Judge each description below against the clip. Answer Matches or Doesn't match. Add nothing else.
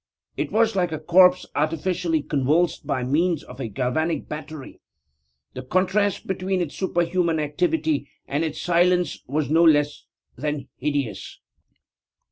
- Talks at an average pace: Doesn't match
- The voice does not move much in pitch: Doesn't match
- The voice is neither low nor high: Matches